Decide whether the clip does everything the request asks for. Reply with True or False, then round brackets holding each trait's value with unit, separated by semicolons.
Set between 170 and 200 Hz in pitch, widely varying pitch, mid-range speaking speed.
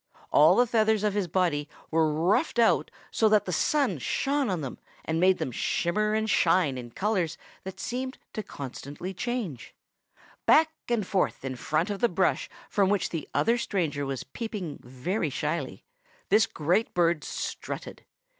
True (185 Hz; 6.0 semitones; 165 wpm)